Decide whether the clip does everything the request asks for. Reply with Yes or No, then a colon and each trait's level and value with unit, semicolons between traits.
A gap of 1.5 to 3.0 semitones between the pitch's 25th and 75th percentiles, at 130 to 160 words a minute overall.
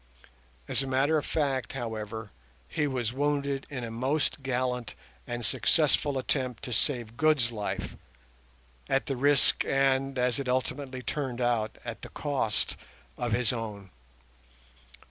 Yes: average, 2.7 semitones; average, 140 wpm